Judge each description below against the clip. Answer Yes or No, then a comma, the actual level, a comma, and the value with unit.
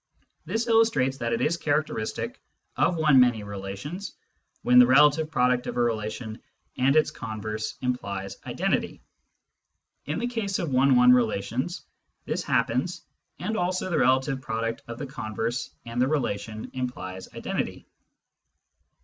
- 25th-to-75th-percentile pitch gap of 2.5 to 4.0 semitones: No, average, 5.1 semitones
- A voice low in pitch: Yes, low, 125 Hz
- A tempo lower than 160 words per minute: Yes, average, 140 wpm